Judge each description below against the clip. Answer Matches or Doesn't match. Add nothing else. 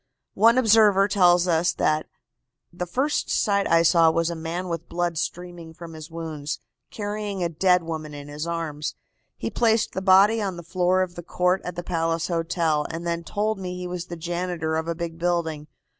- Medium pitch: Matches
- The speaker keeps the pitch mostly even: Matches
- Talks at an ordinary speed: Matches